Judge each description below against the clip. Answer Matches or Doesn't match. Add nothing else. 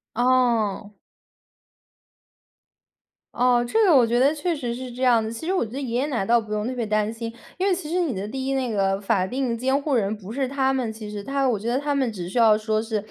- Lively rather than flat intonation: Doesn't match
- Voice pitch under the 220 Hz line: Doesn't match